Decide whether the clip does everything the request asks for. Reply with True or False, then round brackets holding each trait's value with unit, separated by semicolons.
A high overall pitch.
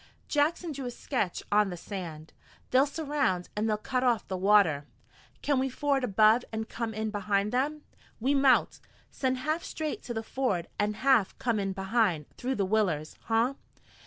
True (225 Hz)